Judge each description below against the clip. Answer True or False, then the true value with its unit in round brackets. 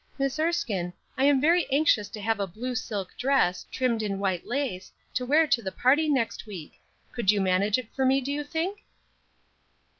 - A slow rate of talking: False (190 wpm)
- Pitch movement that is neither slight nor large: False (5.8 semitones)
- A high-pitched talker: True (250 Hz)